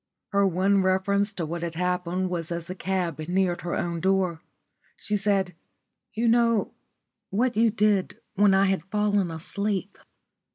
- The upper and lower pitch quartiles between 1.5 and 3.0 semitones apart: Yes, narrow, 2.4 semitones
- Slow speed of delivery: No, average, 155 wpm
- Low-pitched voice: No, high, 190 Hz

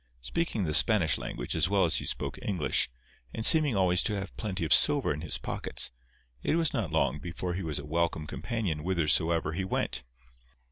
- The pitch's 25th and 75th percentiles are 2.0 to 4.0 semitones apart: No, average, 5.2 semitones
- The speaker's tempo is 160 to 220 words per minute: Yes, average, 190 wpm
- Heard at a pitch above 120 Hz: No, very low, 90 Hz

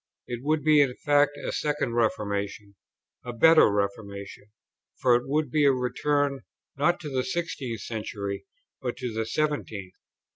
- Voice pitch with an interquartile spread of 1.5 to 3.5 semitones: No, wide, 5.5 semitones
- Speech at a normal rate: Yes, average, 150 wpm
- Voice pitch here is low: Yes, low, 125 Hz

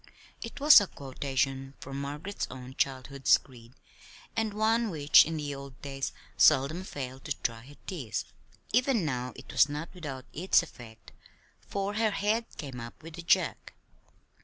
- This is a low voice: No, medium, 145 Hz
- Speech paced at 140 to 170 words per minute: Yes, average, 160 wpm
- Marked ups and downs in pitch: Yes, wide, 6.4 semitones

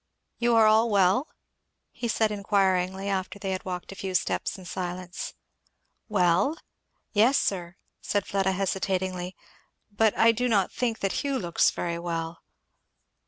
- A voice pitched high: Yes, high, 195 Hz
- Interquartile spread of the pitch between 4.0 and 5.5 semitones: No, average, 3.0 semitones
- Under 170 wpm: Yes, average, 150 wpm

